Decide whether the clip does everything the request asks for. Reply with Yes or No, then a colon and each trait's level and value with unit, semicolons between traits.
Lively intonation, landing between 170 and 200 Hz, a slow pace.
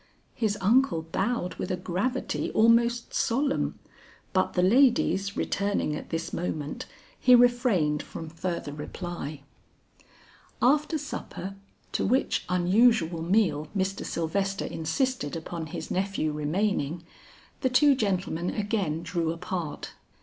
Yes: wide, 6.1 semitones; high, 190 Hz; slow, 115 wpm